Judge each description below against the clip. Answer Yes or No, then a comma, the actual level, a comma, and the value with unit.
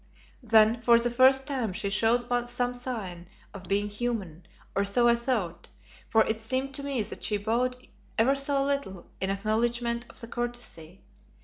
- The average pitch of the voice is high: Yes, high, 235 Hz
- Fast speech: No, average, 170 wpm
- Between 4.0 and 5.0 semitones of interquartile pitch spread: No, average, 3.4 semitones